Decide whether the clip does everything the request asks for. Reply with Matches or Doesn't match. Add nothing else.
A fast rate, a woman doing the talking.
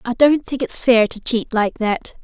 Matches